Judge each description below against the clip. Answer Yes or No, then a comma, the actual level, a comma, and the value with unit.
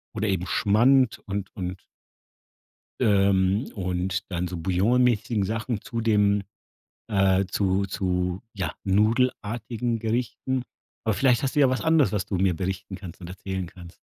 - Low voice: Yes, low, 100 Hz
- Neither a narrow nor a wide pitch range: Yes, average, 3.6 semitones